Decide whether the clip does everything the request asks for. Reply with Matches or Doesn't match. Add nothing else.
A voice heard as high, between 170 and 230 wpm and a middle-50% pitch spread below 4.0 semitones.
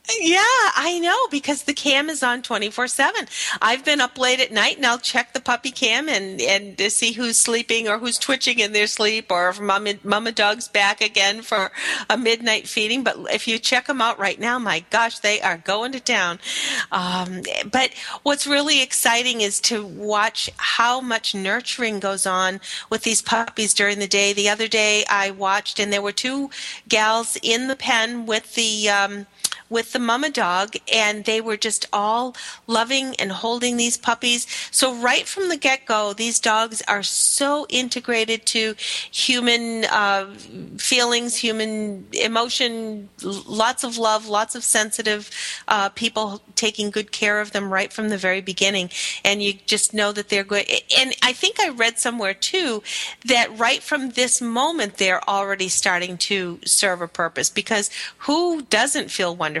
Matches